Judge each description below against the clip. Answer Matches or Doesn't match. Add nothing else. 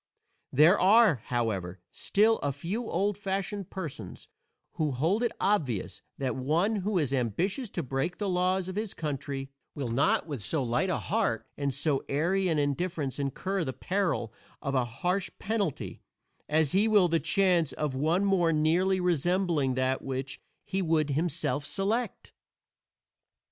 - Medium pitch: Matches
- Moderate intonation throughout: Doesn't match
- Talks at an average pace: Matches